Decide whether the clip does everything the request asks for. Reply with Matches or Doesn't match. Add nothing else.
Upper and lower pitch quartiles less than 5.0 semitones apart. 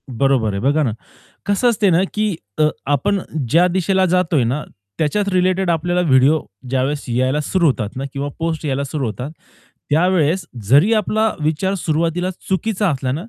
Doesn't match